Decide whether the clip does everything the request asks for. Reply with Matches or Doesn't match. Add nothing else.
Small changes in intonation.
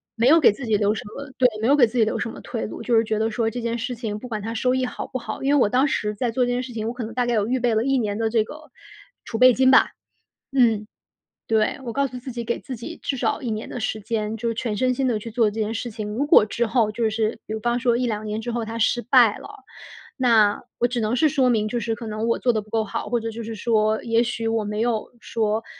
Matches